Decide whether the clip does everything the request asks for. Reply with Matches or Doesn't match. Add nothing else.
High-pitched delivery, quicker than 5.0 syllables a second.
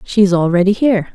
Matches